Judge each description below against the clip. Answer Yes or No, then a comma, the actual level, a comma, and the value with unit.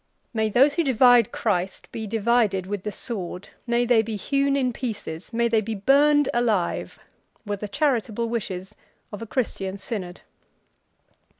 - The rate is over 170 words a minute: No, average, 155 wpm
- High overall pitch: Yes, high, 225 Hz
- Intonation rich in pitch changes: No, average, 3.5 semitones